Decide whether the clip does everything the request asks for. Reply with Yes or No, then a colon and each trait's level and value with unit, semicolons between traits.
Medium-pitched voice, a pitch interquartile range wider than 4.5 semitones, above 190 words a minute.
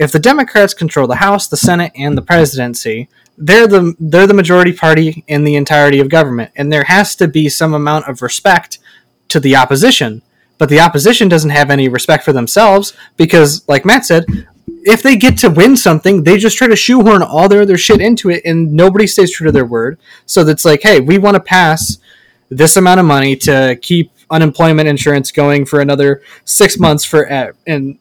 Yes: medium, 160 Hz; average, 5.0 semitones; fast, 205 wpm